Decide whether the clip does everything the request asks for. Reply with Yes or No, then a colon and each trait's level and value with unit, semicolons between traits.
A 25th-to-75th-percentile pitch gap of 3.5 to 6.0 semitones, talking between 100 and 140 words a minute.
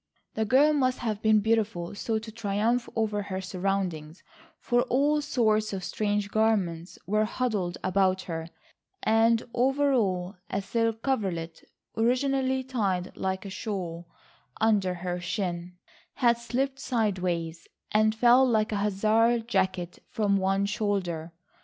Yes: average, 3.8 semitones; slow, 135 wpm